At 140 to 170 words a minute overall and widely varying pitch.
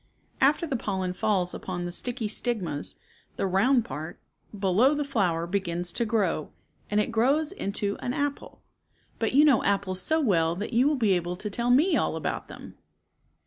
No: average, 180 wpm; wide, 5.9 semitones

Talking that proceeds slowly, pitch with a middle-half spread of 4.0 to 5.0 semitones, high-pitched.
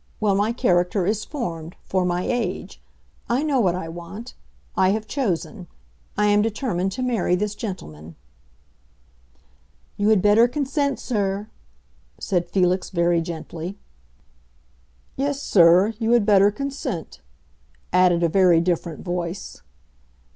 Yes: slow, 125 wpm; average, 4.3 semitones; high, 195 Hz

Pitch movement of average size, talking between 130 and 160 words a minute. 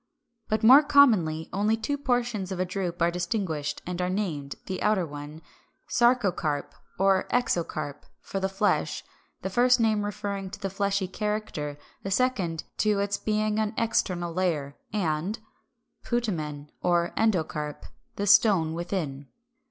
Yes: average, 4.5 semitones; average, 140 wpm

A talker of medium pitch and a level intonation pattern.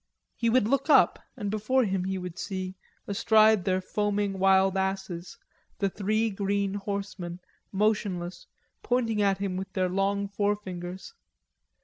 No: high, 195 Hz; narrow, 1.8 semitones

